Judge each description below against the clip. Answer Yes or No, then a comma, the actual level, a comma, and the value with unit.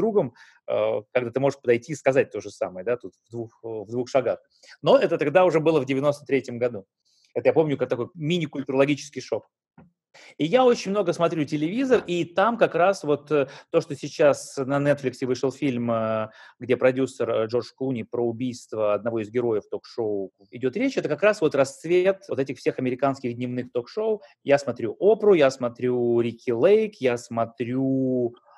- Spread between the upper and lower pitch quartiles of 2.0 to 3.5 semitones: No, average, 4.3 semitones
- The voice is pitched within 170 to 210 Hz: No, low, 135 Hz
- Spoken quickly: Yes, fast, 170 wpm